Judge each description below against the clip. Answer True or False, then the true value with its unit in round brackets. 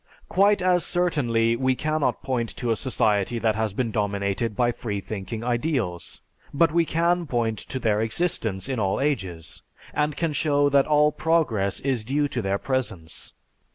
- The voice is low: True (120 Hz)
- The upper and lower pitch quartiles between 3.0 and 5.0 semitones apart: False (5.6 semitones)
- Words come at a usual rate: True (160 wpm)